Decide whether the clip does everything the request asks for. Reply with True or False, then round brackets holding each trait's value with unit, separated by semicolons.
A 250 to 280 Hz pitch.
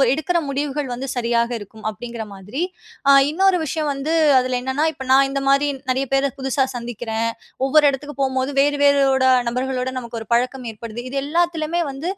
True (270 Hz)